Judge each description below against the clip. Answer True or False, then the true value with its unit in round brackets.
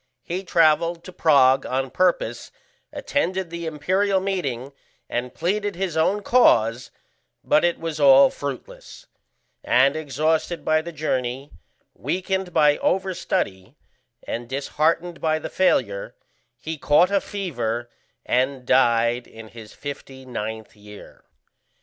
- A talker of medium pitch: True (150 Hz)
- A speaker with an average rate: False (125 wpm)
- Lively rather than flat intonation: True (5.8 semitones)